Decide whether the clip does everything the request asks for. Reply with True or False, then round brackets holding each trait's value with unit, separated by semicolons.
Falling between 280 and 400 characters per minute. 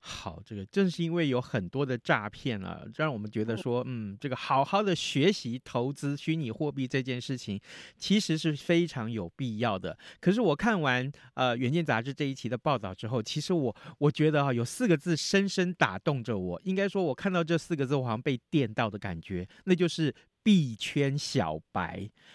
True (295 characters per minute)